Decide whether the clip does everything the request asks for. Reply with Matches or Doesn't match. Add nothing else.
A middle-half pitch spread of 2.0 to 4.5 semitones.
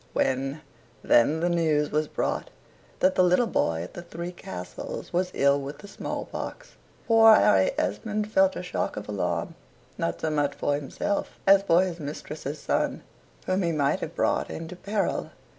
Doesn't match